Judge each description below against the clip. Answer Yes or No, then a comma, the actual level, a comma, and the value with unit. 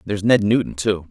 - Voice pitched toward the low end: Yes, low, 100 Hz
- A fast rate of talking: Yes, fast, 220 wpm